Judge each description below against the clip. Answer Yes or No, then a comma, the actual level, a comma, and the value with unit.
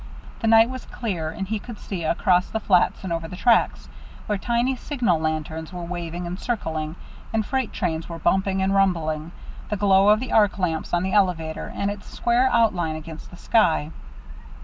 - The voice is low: No, high, 190 Hz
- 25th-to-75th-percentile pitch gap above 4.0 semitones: Yes, average, 4.7 semitones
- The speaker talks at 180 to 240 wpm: Yes, average, 190 wpm